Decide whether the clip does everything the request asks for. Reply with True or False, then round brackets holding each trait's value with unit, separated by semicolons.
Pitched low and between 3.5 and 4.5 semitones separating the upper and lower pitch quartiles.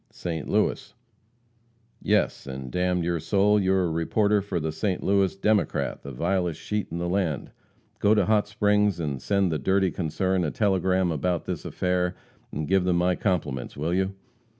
False (90 Hz; 3.1 semitones)